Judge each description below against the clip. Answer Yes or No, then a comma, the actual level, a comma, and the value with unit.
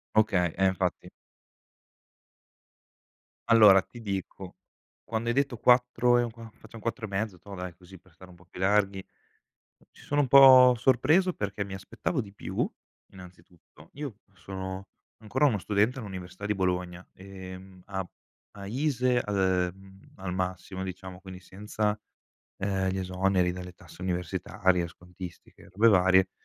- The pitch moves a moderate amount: Yes, average, 3.2 semitones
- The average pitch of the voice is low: Yes, very low, 95 Hz